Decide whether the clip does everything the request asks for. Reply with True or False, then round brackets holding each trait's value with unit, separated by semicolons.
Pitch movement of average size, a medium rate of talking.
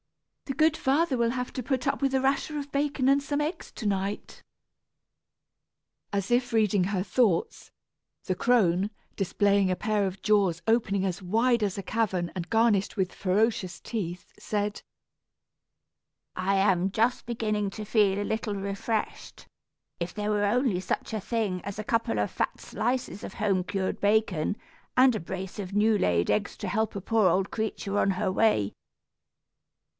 True (3.3 semitones; 170 wpm)